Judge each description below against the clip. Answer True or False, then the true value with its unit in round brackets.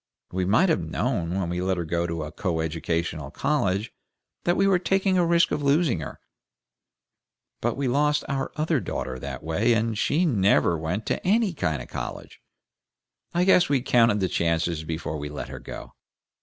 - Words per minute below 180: False (185 wpm)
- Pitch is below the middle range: True (105 Hz)